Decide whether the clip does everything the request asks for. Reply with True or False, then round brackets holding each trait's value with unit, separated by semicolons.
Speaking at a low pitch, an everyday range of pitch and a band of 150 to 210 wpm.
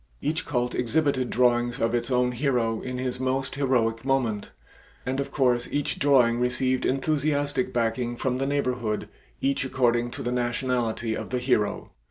False (125 Hz; 2.0 semitones; 160 wpm)